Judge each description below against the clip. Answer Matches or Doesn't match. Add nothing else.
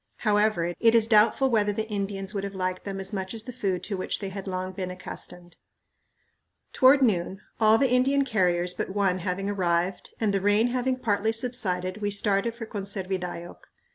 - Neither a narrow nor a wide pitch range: Matches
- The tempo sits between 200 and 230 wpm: Doesn't match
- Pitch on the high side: Matches